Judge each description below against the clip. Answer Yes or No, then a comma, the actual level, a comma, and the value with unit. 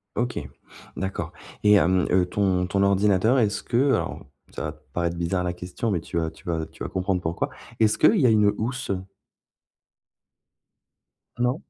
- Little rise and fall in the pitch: No, average, 3.7 semitones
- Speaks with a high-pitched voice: No, very low, 95 Hz